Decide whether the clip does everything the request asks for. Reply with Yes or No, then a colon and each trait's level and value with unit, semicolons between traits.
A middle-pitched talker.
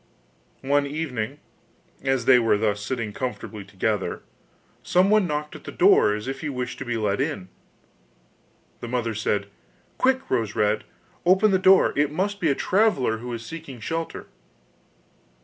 No: low, 130 Hz